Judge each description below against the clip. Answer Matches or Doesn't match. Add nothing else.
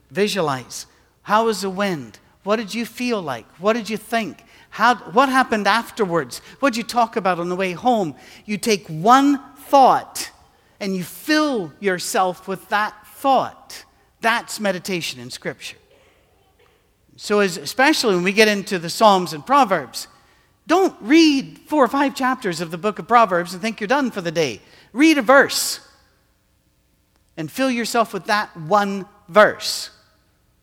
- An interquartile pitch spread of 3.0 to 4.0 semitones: Doesn't match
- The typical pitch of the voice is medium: Doesn't match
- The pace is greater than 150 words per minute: Matches